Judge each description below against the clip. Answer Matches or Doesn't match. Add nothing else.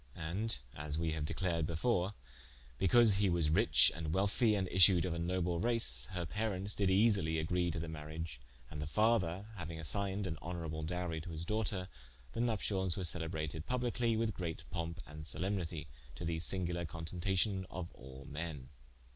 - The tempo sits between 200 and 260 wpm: Doesn't match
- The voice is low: Matches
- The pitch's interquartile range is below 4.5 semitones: Matches